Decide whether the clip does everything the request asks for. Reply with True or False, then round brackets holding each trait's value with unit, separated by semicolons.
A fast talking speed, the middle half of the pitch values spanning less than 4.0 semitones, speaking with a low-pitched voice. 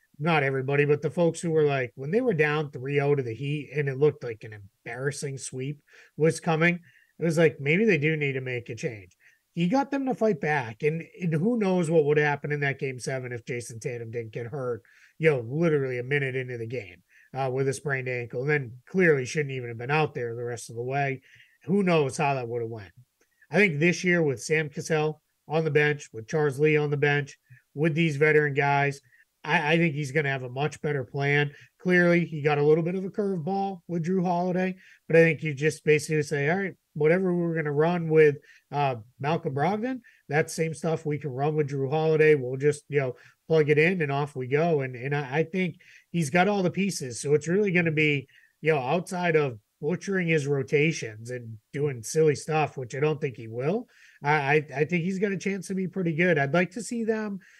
False (230 wpm; 3.4 semitones; 150 Hz)